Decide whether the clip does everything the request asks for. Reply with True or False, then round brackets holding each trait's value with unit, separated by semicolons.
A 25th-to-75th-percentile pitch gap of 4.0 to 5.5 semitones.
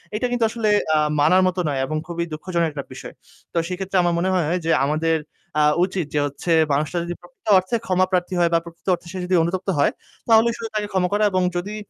False (2.4 semitones)